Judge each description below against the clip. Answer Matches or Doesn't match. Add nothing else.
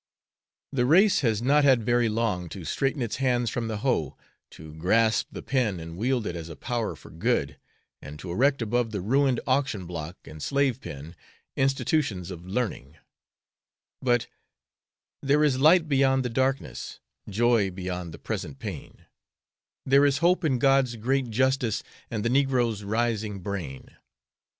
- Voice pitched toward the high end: Doesn't match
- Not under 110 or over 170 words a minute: Matches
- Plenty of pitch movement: Matches